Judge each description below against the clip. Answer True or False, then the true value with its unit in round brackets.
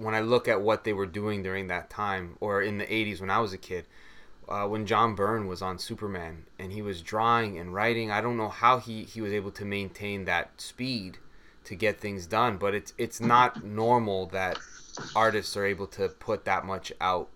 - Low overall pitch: True (105 Hz)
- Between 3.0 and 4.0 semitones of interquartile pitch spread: False (2.6 semitones)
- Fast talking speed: True (220 wpm)